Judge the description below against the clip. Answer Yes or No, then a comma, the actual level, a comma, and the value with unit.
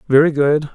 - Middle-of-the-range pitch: Yes, medium, 150 Hz